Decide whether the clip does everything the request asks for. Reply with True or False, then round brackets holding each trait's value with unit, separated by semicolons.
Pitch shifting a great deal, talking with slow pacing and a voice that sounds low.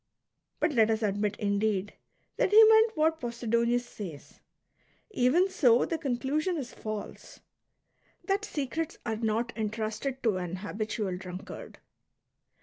False (6.0 semitones; 130 wpm; 235 Hz)